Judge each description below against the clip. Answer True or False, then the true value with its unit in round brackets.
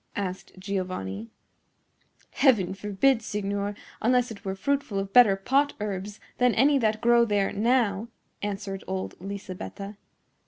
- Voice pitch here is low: False (205 Hz)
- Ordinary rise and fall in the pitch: True (3.4 semitones)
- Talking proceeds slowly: True (125 wpm)